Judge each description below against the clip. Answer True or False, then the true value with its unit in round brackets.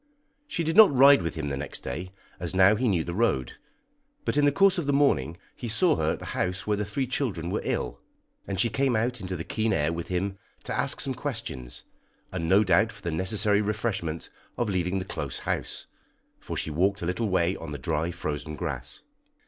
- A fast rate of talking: True (215 wpm)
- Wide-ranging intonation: True (6.1 semitones)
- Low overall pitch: True (95 Hz)